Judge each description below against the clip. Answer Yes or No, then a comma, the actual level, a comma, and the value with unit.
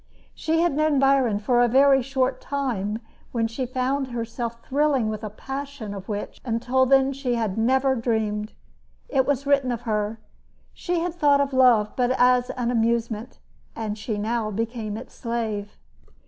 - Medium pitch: No, high, 245 Hz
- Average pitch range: Yes, average, 3.3 semitones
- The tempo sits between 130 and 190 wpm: Yes, average, 165 wpm